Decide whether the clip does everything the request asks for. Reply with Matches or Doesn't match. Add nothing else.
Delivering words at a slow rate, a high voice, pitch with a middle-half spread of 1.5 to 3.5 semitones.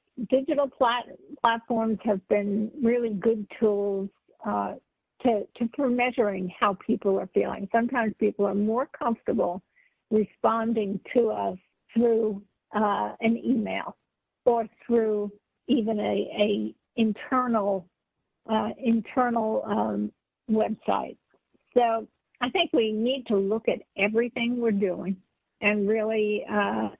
Matches